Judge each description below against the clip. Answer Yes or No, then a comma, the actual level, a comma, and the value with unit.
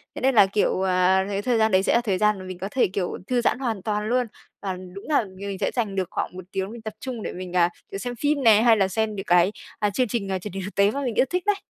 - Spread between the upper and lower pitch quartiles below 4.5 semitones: Yes, average, 3.8 semitones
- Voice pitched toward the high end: Yes, high, 205 Hz